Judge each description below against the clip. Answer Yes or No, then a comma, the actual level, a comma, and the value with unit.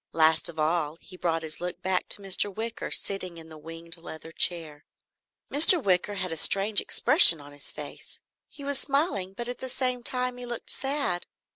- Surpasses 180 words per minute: Yes, average, 190 wpm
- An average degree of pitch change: No, wide, 6.9 semitones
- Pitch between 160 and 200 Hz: Yes, medium, 185 Hz